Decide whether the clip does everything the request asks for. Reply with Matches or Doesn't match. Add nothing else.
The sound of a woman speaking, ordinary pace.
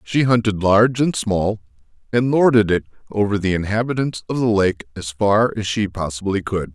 Doesn't match